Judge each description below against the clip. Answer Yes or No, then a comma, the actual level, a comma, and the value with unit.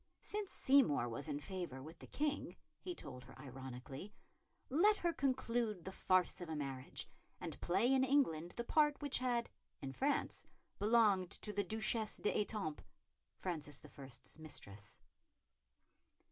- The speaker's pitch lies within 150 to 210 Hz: Yes, high, 190 Hz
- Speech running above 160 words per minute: No, average, 140 wpm